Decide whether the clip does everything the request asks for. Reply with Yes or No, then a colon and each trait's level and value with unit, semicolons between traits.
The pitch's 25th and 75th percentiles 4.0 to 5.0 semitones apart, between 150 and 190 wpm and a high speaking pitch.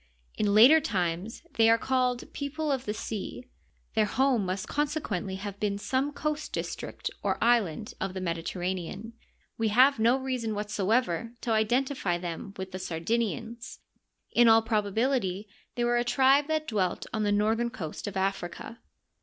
Yes: average, 4.4 semitones; average, 160 wpm; high, 225 Hz